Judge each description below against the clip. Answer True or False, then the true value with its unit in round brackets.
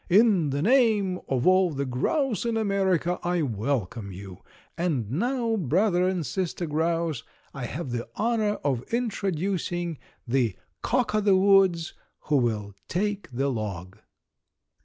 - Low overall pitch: False (175 Hz)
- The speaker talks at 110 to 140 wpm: True (135 wpm)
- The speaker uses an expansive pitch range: True (7.2 semitones)